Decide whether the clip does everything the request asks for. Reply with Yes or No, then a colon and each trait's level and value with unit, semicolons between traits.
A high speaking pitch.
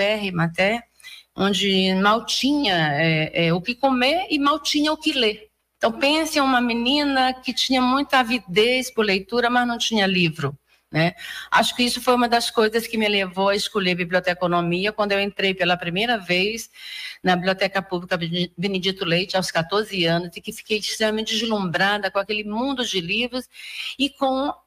Yes: high, 215 Hz